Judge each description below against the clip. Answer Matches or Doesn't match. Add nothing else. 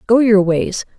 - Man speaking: Doesn't match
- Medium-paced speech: Matches